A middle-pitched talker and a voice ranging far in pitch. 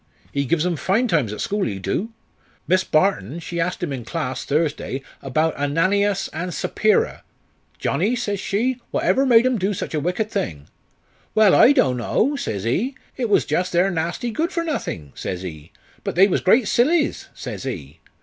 Yes: medium, 180 Hz; wide, 7.8 semitones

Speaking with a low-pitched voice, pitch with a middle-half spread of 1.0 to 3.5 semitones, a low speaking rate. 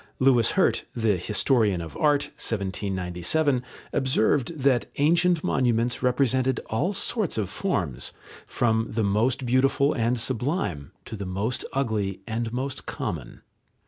No: low, 120 Hz; average, 4.7 semitones; slow, 125 wpm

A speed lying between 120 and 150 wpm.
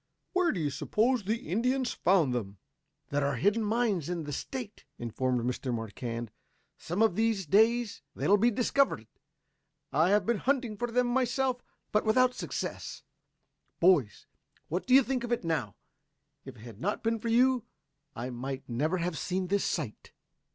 No: average, 170 wpm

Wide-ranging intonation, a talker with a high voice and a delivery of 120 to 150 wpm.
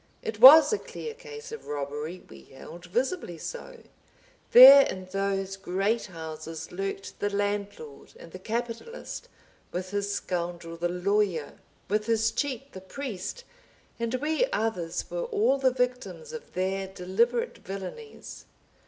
Yes: wide, 6.4 semitones; high, 205 Hz; slow, 135 wpm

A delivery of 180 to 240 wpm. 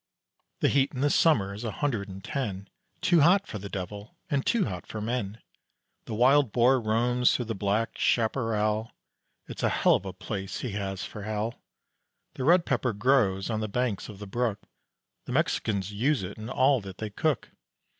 Yes: average, 195 wpm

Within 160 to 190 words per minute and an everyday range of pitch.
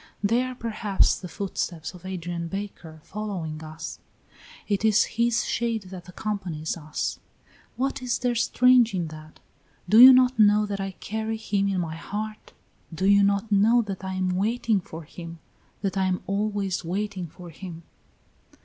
Yes: average, 165 wpm; average, 3.8 semitones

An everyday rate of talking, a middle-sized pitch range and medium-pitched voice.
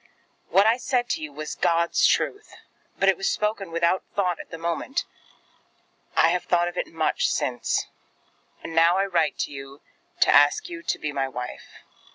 Yes: average, 175 wpm; average, 4.3 semitones; medium, 170 Hz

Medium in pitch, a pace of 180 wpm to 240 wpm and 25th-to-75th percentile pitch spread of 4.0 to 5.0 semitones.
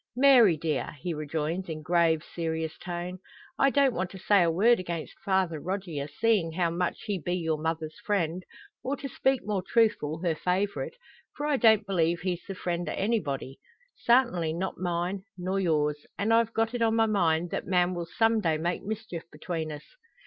Yes: medium, 180 Hz; average, 185 wpm; average, 4.7 semitones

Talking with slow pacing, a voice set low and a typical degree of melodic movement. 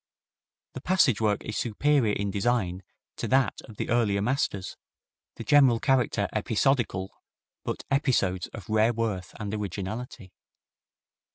Yes: slow, 125 wpm; low, 110 Hz; average, 4.0 semitones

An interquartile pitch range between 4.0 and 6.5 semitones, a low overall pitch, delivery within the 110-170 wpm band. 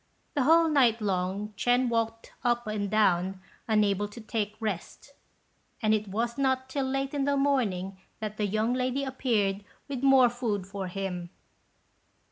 No: average, 4.4 semitones; high, 225 Hz; average, 155 wpm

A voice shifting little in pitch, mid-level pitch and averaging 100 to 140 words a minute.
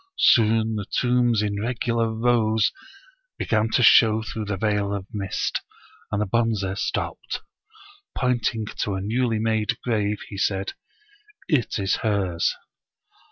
No: narrow, 2.3 semitones; low, 110 Hz; slow, 135 wpm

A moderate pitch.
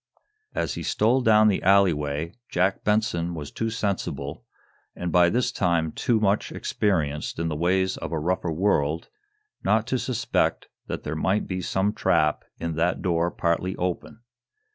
No: very low, 90 Hz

